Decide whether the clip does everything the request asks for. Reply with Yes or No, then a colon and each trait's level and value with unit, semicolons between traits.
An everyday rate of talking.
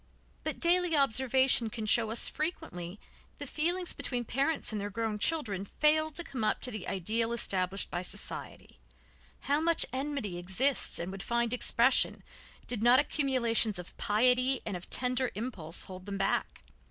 Yes: average, 165 wpm